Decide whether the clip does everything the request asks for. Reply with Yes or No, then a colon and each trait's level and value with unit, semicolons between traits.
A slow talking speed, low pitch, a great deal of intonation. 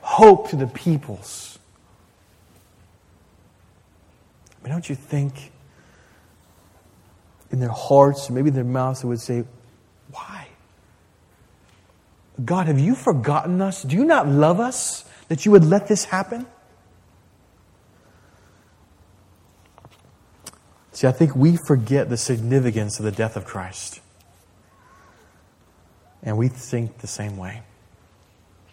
Yes: slow, 115 wpm; low, 110 Hz; wide, 7.1 semitones